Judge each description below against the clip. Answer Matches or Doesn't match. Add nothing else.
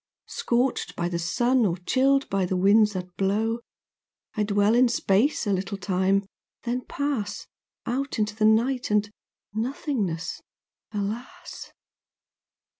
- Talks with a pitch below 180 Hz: Doesn't match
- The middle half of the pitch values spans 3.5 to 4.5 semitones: Matches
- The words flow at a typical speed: Doesn't match